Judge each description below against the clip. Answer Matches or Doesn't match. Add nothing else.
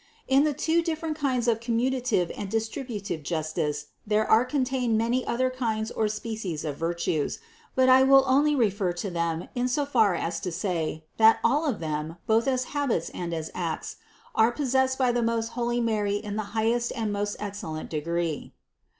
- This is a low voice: Doesn't match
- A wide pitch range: Matches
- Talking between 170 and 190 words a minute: Matches